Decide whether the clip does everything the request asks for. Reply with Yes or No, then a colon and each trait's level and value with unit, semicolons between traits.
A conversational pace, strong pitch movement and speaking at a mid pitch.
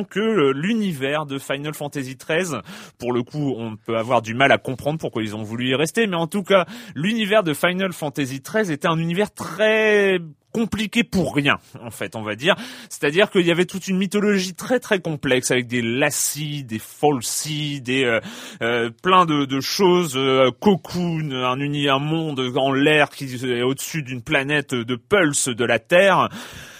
Yes: average, 185 wpm; wide, 6.1 semitones; medium, 150 Hz